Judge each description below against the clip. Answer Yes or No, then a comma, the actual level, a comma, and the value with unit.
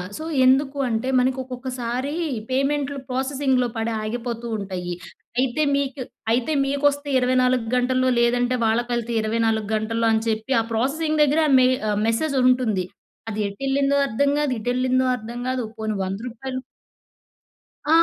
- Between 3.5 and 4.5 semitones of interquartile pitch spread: No, average, 2.9 semitones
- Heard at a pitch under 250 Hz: No, very high, 255 Hz